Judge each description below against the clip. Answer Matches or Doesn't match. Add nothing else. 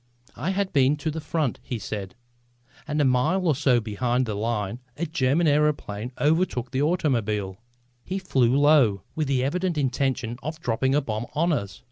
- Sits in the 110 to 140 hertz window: Matches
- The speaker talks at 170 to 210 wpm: Matches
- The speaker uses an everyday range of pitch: Matches